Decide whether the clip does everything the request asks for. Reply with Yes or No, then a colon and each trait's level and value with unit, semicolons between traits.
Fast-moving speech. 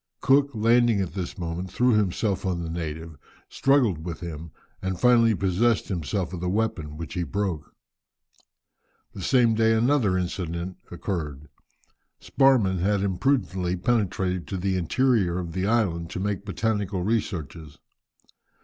No: average, 140 wpm